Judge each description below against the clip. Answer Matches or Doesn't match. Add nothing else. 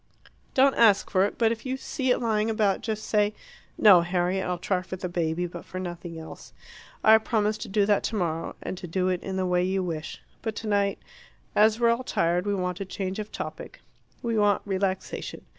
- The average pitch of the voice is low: Doesn't match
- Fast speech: Matches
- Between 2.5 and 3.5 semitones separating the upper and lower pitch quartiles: Matches